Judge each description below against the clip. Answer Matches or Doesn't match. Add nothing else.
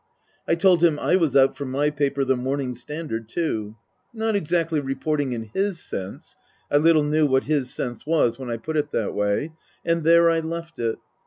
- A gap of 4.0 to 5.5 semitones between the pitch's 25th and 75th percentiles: Matches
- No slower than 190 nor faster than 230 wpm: Matches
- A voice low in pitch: Doesn't match